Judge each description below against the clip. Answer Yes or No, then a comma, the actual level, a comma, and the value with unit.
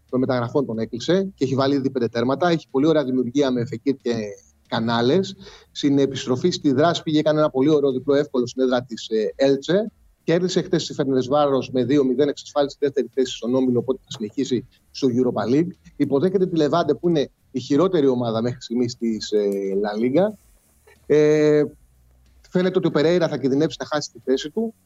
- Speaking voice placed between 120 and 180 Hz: Yes, low, 135 Hz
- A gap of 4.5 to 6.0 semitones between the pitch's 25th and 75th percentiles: No, average, 3.9 semitones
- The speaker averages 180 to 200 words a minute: Yes, fast, 185 wpm